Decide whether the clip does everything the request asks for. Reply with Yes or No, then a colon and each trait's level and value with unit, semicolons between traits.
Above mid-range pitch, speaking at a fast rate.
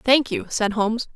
Yes: high, 235 Hz; fast, 210 wpm